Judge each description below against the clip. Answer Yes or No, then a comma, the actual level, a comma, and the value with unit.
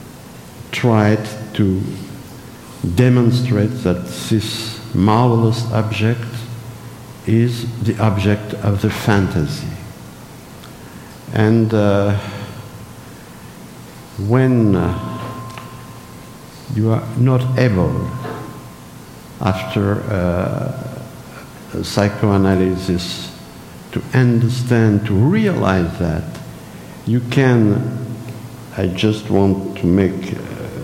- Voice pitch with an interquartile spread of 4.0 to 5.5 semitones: No, average, 3.4 semitones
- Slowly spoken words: Yes, slow, 70 wpm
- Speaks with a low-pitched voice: Yes, low, 110 Hz